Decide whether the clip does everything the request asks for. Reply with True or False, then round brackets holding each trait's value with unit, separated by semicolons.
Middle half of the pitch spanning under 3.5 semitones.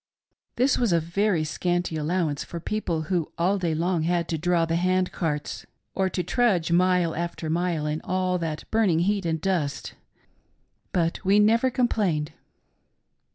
True (2.5 semitones)